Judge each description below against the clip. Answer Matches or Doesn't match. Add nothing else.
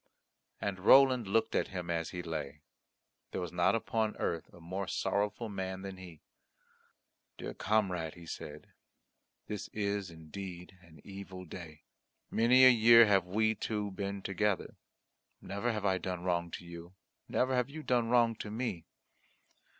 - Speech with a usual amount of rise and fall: Matches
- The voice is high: Doesn't match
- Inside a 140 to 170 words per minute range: Matches